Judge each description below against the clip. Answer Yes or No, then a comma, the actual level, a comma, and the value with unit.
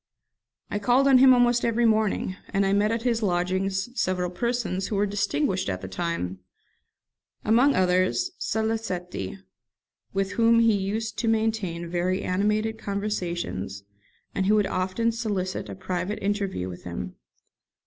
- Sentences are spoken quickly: No, average, 145 wpm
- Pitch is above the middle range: Yes, high, 200 Hz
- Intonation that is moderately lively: Yes, average, 3.5 semitones